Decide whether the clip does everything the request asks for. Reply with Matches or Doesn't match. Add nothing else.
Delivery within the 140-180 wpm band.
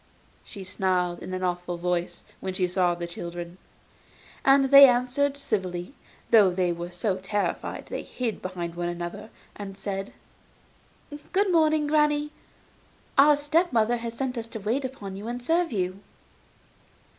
Matches